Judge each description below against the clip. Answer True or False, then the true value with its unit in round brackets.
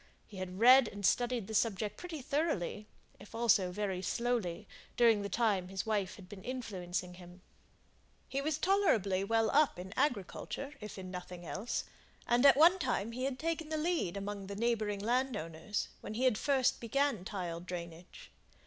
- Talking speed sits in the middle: True (165 wpm)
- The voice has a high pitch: True (215 Hz)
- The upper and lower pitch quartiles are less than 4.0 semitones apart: False (5.5 semitones)